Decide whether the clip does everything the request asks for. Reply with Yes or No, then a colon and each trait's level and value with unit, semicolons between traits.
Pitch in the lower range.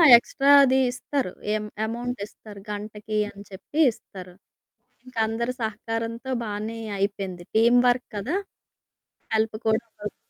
No: high, 220 Hz